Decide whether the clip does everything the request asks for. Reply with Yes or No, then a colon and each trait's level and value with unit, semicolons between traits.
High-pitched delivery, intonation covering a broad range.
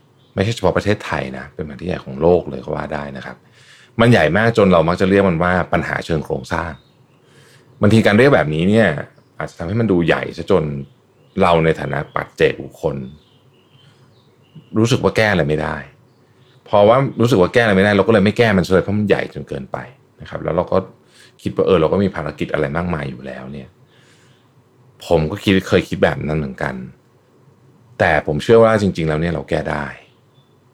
No: very low, 95 Hz; wide, 7.3 semitones